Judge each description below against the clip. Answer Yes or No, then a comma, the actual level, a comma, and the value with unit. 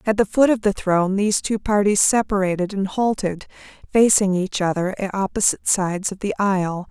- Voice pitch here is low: No, high, 200 Hz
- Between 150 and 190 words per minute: Yes, average, 180 wpm